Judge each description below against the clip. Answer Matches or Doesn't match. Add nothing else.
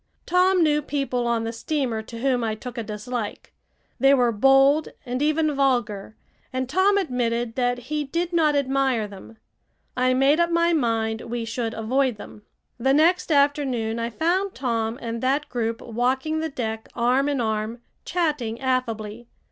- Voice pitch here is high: Matches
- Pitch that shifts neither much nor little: Matches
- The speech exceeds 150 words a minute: Matches